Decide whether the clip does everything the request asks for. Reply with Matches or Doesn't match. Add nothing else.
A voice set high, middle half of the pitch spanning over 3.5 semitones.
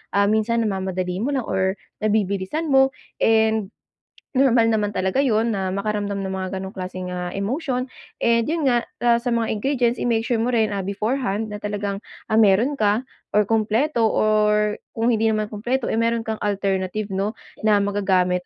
Doesn't match